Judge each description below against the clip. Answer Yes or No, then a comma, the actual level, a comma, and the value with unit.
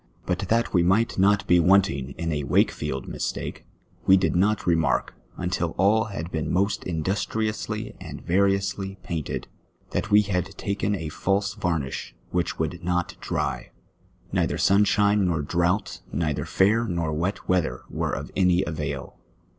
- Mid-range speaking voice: No, very low, 90 Hz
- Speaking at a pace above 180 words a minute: No, average, 145 wpm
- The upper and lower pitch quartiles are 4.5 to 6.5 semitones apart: No, average, 3.1 semitones